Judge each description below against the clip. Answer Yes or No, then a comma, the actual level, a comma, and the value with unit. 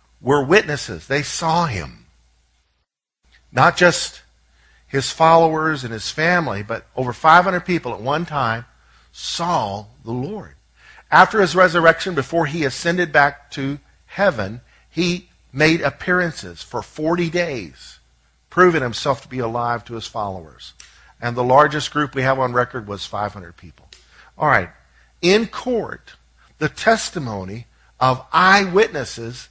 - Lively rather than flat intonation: Yes, wide, 7.1 semitones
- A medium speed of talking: No, slow, 130 wpm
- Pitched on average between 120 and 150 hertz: Yes, low, 135 Hz